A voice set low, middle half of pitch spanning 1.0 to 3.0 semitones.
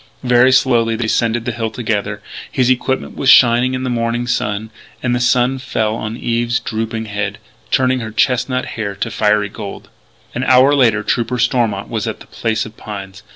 Yes: low, 115 Hz; narrow, 2.5 semitones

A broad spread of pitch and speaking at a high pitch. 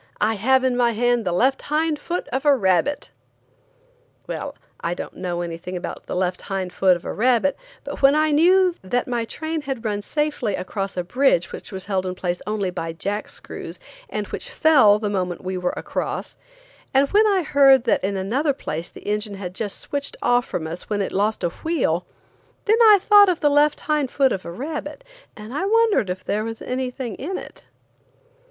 Yes: wide, 7.5 semitones; high, 230 Hz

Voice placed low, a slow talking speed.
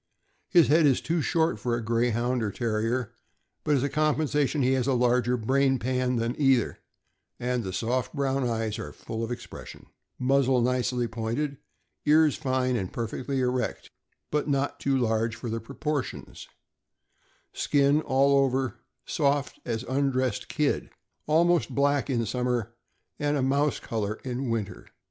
No: low, 130 Hz; average, 155 wpm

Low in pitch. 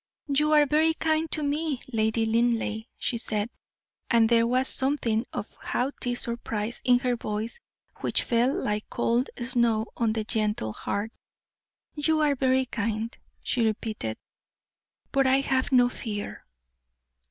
No: high, 240 Hz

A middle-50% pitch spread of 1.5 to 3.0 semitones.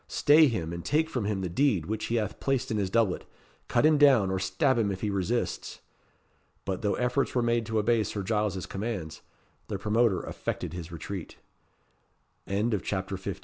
No: average, 3.9 semitones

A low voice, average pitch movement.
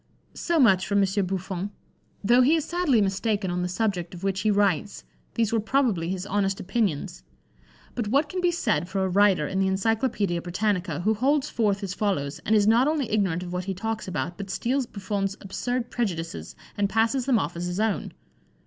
No: high, 200 Hz; average, 3.7 semitones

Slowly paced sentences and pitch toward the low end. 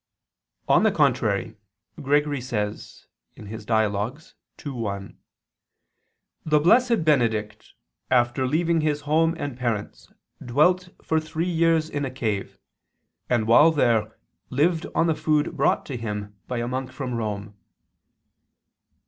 Yes: slow, 125 wpm; low, 130 Hz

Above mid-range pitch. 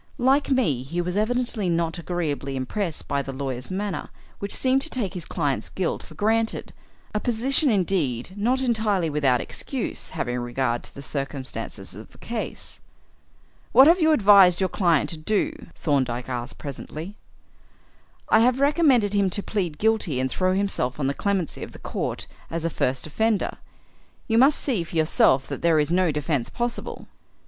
No: medium, 180 Hz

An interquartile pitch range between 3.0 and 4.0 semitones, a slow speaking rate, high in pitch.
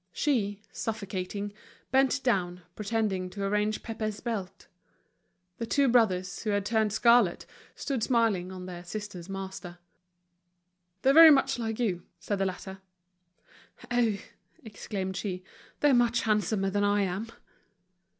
Yes: average, 3.3 semitones; slow, 130 wpm; high, 205 Hz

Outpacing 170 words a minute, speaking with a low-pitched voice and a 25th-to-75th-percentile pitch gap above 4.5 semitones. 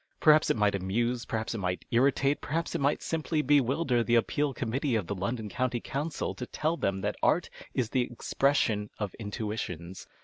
Yes: average, 180 wpm; low, 120 Hz; average, 5.2 semitones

